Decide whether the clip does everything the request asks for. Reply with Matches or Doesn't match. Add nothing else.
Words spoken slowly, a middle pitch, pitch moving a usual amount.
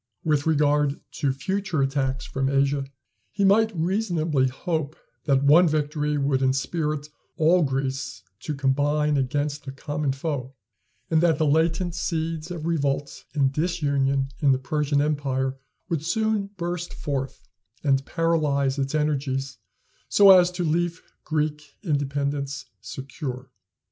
Matches